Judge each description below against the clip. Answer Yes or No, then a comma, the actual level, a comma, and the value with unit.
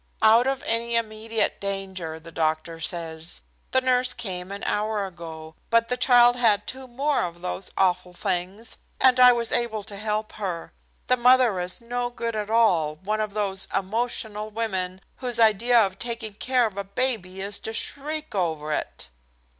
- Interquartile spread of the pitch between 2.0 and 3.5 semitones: No, average, 4.4 semitones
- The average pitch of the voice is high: Yes, high, 215 Hz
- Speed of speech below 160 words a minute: No, average, 170 wpm